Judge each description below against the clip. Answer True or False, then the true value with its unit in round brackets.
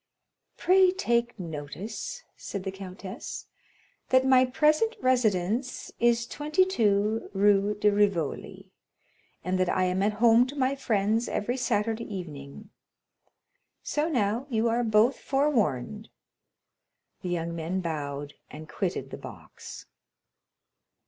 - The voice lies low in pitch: False (215 Hz)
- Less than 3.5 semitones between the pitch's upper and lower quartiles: False (5.5 semitones)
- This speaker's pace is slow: True (115 wpm)